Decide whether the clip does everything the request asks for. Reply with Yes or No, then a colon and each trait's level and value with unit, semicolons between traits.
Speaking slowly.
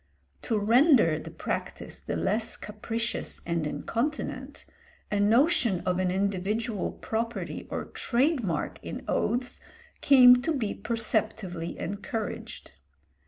Yes: slow, 115 wpm